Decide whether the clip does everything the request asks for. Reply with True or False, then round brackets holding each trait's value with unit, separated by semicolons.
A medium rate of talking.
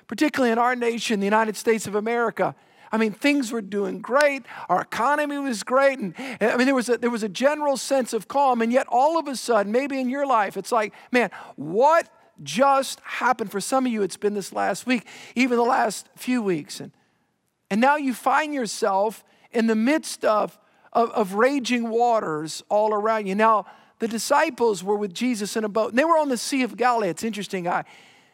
False (210 wpm)